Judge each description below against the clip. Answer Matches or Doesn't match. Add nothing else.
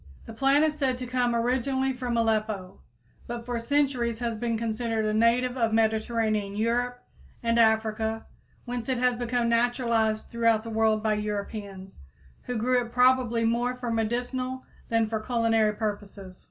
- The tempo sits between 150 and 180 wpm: Matches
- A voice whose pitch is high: Matches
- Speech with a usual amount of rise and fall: Doesn't match